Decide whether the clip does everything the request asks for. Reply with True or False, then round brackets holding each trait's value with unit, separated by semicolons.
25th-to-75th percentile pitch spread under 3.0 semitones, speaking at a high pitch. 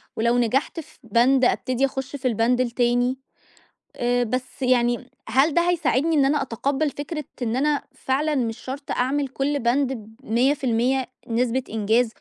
True (2.6 semitones; 255 Hz)